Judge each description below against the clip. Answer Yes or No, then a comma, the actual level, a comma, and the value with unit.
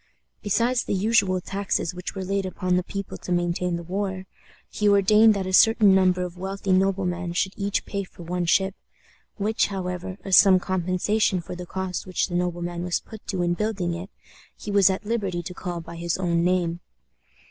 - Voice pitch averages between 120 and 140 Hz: No, medium, 185 Hz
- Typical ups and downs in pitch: No, narrow, 2.0 semitones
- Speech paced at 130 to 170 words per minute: No, average, 190 wpm